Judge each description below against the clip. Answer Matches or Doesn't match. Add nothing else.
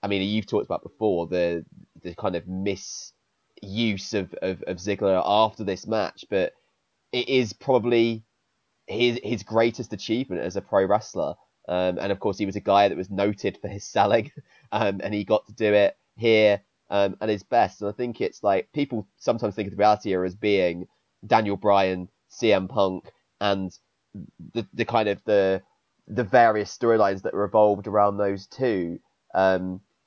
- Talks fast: Doesn't match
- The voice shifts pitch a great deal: Doesn't match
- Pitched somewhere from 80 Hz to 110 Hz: Matches